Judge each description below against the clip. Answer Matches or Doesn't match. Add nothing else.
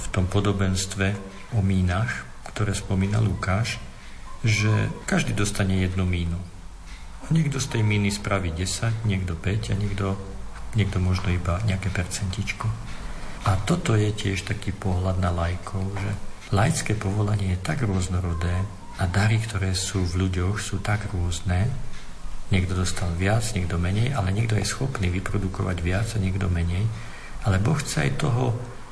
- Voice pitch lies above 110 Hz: Doesn't match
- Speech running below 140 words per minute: Doesn't match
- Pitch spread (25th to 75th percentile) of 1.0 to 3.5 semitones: Matches